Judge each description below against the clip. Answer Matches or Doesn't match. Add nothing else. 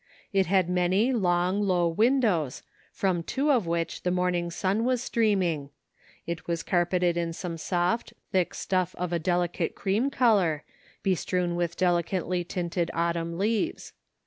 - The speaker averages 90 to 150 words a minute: Matches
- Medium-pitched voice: Matches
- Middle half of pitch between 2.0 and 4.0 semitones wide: Matches